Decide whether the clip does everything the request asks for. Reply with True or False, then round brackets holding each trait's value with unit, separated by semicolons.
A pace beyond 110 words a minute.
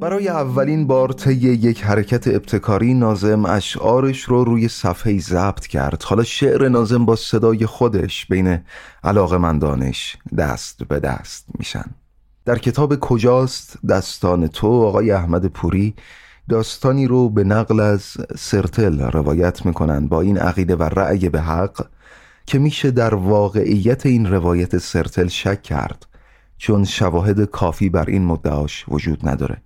True (135 wpm)